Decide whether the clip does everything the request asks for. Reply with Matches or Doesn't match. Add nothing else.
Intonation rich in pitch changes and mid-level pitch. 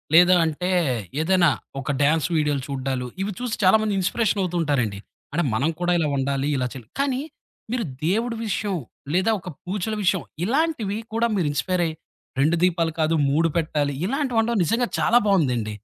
Matches